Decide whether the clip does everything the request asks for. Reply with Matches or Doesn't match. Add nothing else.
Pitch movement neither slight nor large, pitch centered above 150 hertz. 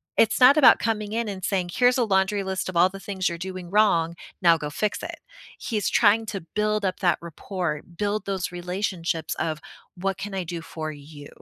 Matches